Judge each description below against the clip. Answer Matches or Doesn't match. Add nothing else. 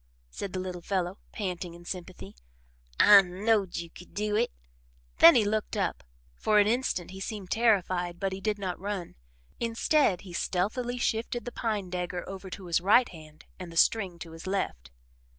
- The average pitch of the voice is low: Doesn't match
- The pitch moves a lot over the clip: Doesn't match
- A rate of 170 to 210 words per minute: Matches